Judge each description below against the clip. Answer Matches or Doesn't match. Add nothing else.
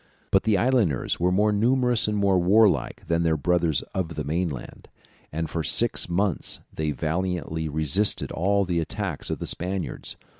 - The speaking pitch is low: Matches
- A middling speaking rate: Matches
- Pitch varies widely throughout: Doesn't match